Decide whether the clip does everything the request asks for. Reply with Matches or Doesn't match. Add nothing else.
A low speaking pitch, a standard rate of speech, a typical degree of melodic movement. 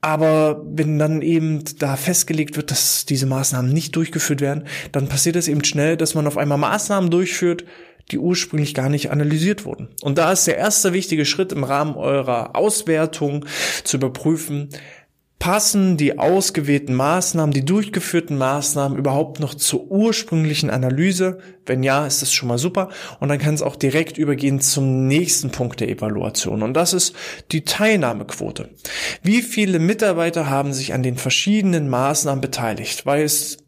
Doesn't match